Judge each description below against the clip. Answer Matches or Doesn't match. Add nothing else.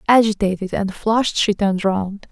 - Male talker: Doesn't match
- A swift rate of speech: Doesn't match